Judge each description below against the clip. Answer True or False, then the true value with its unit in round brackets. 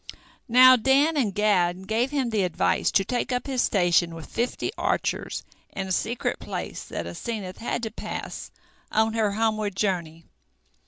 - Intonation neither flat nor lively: True (4.3 semitones)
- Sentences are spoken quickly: False (160 wpm)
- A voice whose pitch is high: True (215 Hz)